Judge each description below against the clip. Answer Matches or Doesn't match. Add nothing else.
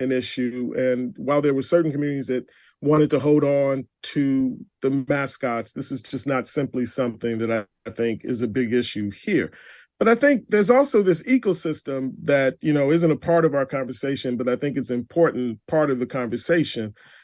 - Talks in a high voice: Doesn't match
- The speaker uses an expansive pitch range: Doesn't match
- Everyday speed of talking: Matches